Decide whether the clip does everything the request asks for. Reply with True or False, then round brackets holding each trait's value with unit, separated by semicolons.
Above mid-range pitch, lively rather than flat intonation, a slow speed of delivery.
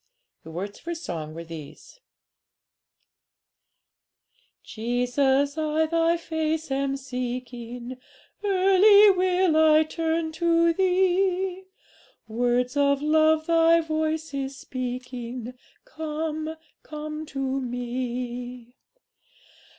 False (300 Hz; 4.8 semitones; 90 wpm)